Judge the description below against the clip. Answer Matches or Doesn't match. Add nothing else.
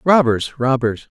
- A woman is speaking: Doesn't match